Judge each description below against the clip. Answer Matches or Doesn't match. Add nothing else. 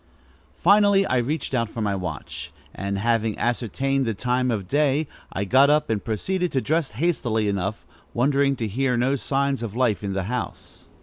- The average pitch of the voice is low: Matches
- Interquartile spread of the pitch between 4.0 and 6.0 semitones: Matches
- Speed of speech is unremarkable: Matches